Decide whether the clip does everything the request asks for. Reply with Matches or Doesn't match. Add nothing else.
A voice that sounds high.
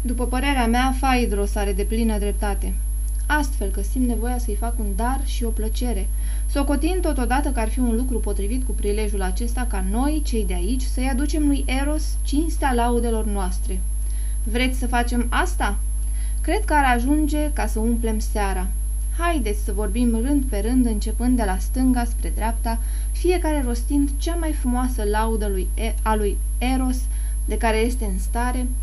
Matches